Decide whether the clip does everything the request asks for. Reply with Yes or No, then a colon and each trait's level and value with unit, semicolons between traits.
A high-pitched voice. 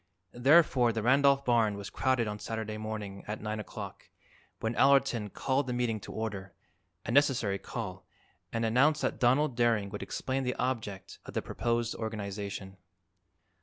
No: low, 115 Hz